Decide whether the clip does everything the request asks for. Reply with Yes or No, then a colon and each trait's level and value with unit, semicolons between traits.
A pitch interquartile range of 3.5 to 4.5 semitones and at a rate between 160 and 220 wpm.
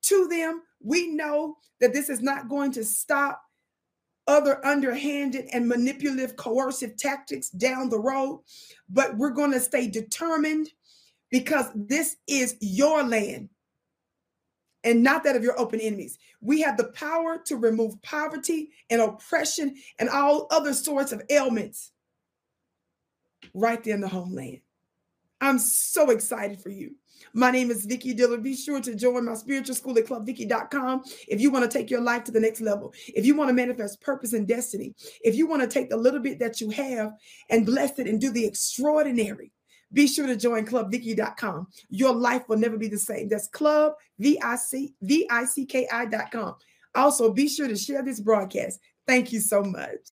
Yes: average, 3.9 semitones; average, 170 wpm